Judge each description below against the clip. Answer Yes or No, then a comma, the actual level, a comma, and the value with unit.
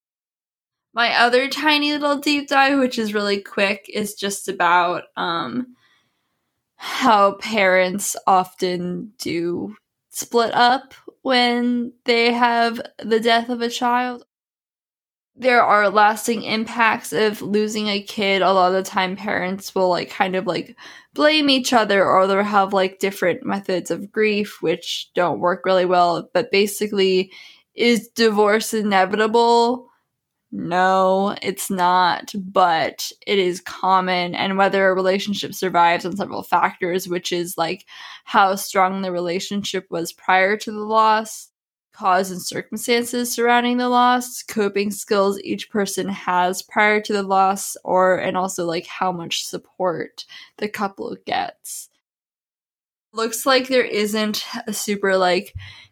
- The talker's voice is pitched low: No, high, 205 Hz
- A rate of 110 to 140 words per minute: Yes, slow, 135 wpm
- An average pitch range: Yes, average, 4.0 semitones